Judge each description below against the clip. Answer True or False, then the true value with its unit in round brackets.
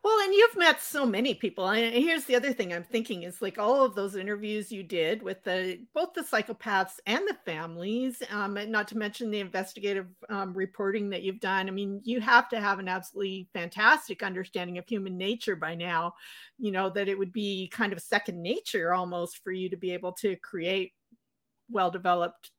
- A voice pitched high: True (200 Hz)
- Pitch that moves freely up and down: False (3.7 semitones)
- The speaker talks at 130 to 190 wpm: False (200 wpm)